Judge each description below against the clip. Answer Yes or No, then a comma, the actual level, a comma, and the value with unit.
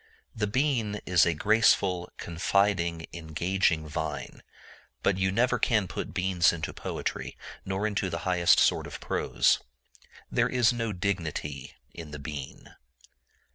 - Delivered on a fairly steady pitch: No, average, 3.8 semitones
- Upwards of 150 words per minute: No, slow, 135 wpm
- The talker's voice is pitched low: Yes, very low, 95 Hz